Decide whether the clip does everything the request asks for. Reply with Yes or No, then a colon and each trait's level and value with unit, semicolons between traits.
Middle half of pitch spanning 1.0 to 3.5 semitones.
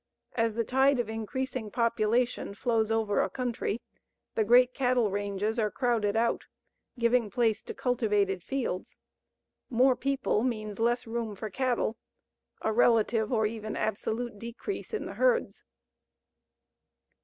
Yes: narrow, 2.4 semitones